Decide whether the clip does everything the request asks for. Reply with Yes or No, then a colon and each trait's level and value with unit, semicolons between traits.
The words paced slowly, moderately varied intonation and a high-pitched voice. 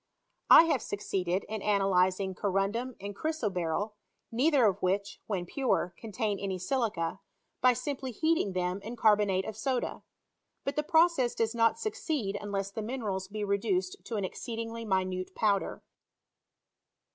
No: average, 145 wpm; average, 4.4 semitones; high, 210 Hz